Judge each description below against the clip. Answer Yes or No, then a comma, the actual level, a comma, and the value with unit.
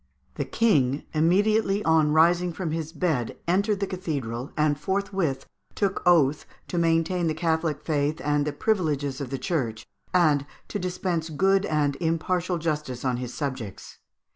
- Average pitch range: Yes, average, 3.9 semitones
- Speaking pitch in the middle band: Yes, medium, 160 Hz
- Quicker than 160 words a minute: No, average, 150 wpm